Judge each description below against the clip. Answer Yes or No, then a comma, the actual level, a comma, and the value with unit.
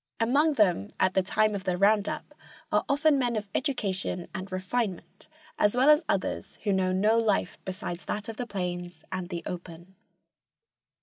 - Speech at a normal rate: Yes, average, 175 wpm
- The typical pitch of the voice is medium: No, high, 200 Hz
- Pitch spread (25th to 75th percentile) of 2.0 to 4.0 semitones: Yes, average, 3.7 semitones